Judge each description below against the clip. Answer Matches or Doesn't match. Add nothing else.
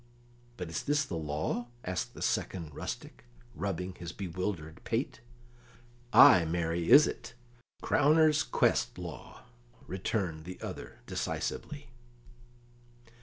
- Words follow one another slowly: Matches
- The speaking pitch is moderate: Doesn't match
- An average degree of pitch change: Doesn't match